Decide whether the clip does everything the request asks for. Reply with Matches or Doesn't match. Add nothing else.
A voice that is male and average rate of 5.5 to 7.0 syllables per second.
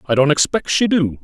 Matches